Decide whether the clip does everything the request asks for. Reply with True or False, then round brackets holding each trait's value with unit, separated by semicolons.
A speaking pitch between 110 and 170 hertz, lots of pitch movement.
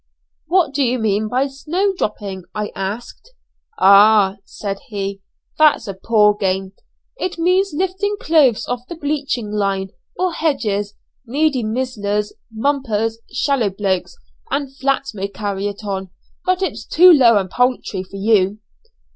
False (225 Hz; 6.0 semitones)